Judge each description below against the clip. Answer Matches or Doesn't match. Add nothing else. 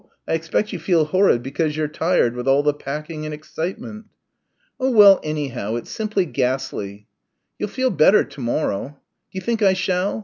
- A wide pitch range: Matches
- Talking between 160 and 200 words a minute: Matches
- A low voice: Doesn't match